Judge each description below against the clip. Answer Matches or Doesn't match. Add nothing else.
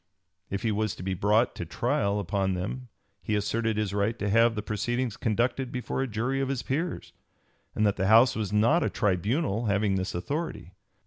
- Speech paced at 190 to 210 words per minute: Matches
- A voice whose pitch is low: Matches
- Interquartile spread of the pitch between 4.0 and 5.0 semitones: Doesn't match